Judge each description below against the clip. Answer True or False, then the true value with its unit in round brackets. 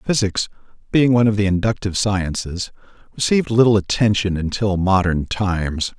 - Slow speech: True (130 wpm)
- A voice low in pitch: True (100 Hz)